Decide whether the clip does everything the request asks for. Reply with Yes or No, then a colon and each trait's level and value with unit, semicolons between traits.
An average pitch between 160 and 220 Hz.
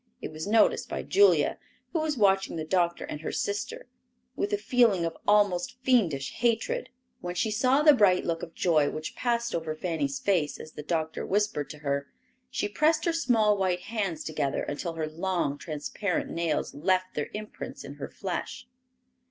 Yes: medium, 185 Hz